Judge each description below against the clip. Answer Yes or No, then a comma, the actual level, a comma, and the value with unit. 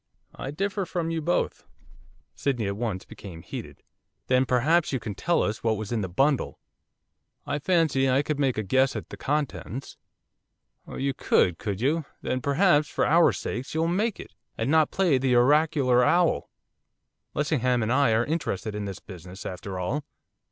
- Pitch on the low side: Yes, low, 130 Hz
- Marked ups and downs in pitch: Yes, wide, 5.8 semitones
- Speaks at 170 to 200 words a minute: Yes, average, 175 wpm